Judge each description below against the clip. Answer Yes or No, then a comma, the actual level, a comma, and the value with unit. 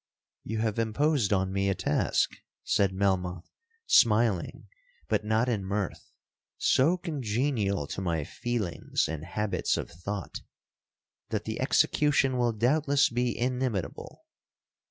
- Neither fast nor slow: No, slow, 120 wpm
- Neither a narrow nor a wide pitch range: Yes, average, 4.5 semitones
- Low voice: Yes, low, 110 Hz